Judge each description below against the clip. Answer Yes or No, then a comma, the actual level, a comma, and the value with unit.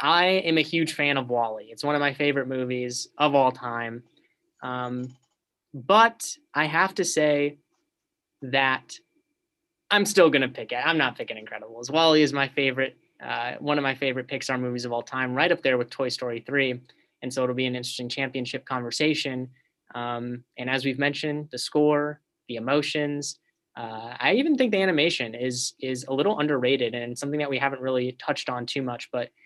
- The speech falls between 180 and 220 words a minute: Yes, average, 190 wpm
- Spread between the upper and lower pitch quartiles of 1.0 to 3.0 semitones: No, average, 3.5 semitones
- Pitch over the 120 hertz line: Yes, low, 135 Hz